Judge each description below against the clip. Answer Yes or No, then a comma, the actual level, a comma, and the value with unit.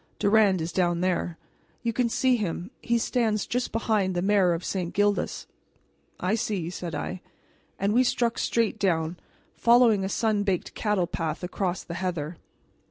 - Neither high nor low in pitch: No, high, 195 Hz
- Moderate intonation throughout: Yes, average, 4.0 semitones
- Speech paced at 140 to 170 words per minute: Yes, average, 165 wpm